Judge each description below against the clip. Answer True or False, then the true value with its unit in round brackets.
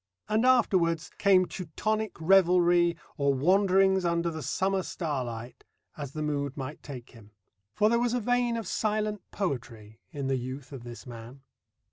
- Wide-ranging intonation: True (6.6 semitones)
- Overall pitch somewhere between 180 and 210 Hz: False (170 Hz)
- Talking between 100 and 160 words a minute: True (155 wpm)